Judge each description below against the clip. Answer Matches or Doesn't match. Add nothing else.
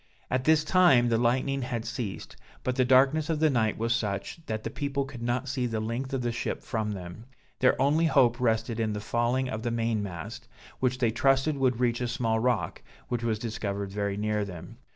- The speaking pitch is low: Matches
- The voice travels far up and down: Doesn't match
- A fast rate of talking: Matches